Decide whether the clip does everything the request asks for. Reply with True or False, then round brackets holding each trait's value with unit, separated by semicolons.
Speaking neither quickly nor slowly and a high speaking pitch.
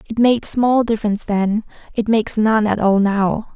True (185 wpm; 215 Hz)